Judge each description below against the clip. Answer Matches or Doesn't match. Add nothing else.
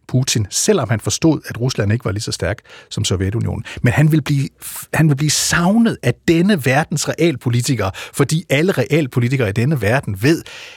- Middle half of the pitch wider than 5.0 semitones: Matches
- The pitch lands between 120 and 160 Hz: Matches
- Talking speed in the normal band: Matches